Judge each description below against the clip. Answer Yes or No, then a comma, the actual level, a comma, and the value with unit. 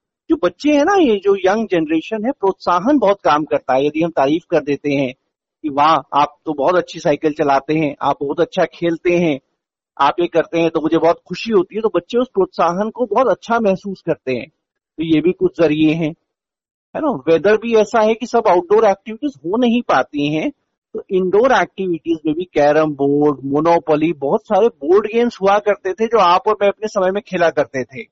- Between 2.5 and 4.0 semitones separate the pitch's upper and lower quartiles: No, average, 5.2 semitones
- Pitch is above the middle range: No, medium, 175 Hz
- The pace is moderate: No, fast, 210 wpm